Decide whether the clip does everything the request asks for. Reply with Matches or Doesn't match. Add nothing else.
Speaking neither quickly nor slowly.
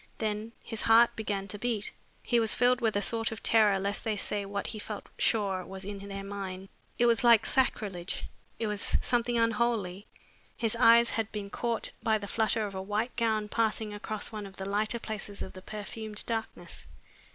Matches